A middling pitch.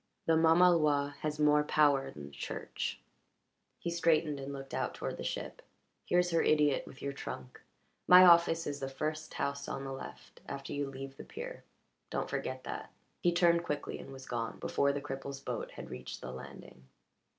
Yes: medium, 145 Hz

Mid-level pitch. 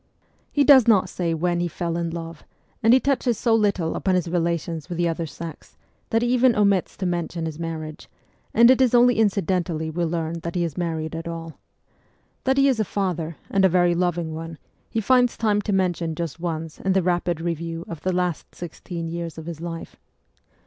Yes: medium, 175 Hz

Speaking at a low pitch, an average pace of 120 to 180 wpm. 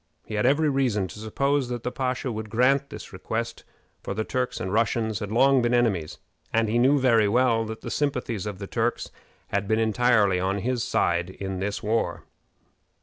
No: low, 115 Hz; average, 195 wpm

